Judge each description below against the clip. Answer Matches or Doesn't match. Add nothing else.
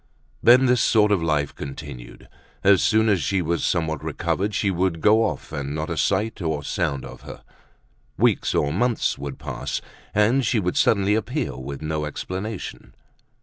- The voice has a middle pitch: Doesn't match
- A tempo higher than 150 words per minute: Matches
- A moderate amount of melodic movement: Doesn't match